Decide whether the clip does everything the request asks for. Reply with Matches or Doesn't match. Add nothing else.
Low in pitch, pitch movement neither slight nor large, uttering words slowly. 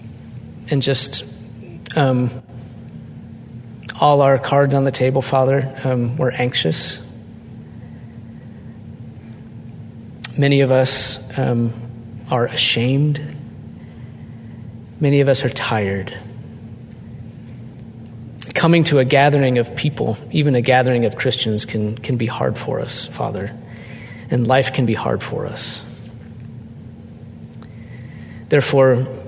Doesn't match